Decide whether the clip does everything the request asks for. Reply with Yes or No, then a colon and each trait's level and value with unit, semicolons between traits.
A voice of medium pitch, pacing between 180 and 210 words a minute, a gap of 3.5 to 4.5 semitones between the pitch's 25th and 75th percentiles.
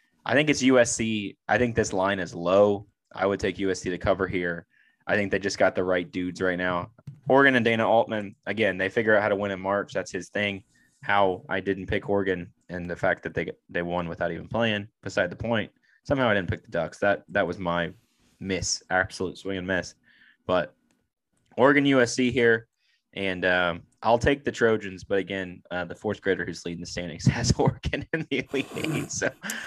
No: low, 100 Hz; fast, 205 wpm; average, 3.8 semitones